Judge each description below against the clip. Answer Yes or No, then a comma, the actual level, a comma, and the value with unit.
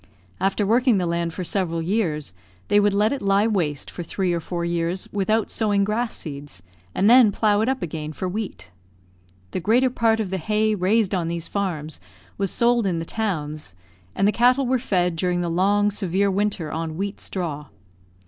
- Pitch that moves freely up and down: No, average, 4.1 semitones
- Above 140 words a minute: Yes, average, 190 wpm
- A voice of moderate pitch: No, high, 195 Hz